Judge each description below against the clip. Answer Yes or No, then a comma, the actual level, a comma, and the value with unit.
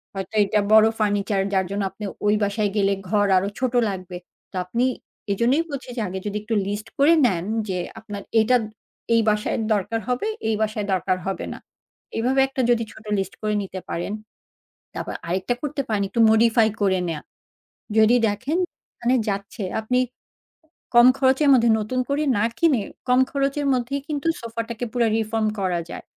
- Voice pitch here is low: No, high, 220 Hz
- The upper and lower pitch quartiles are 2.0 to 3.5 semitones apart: No, average, 3.9 semitones